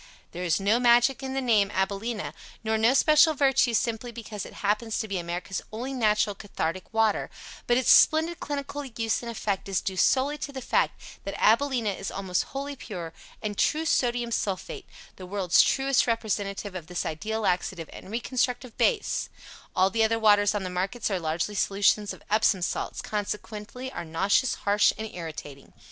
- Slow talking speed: No, average, 175 wpm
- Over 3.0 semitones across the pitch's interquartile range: Yes, average, 4.0 semitones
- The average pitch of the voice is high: Yes, high, 215 Hz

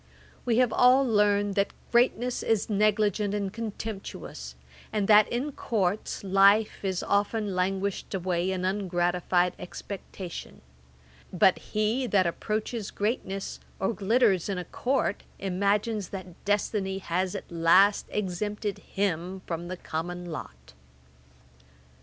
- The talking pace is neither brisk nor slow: No, slow, 120 wpm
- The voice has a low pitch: No, high, 200 Hz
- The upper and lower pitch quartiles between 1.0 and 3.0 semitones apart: Yes, narrow, 2.6 semitones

